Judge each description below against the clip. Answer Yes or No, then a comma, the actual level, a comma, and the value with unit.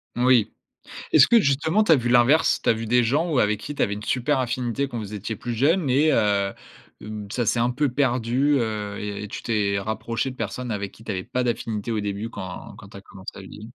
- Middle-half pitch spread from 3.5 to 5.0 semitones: Yes, average, 3.8 semitones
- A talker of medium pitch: No, low, 115 Hz